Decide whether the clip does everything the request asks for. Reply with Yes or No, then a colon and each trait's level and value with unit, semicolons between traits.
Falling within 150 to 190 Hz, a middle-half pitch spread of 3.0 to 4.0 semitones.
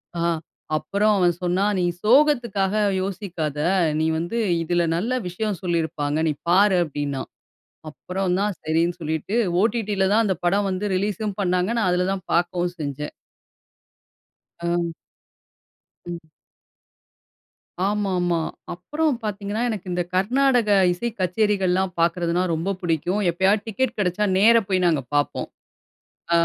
Yes: medium, 185 Hz; average, 3.3 semitones